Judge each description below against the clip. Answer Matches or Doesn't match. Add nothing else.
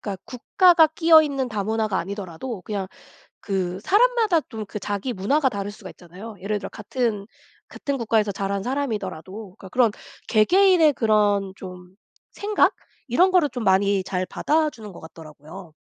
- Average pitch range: Doesn't match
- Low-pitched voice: Doesn't match